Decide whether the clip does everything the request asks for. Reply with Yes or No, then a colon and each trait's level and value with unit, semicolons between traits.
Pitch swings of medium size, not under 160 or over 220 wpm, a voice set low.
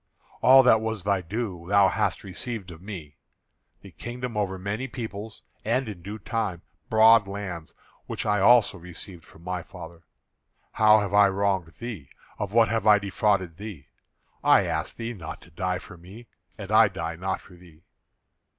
Yes: average, 3.7 semitones; average, 170 wpm; low, 100 Hz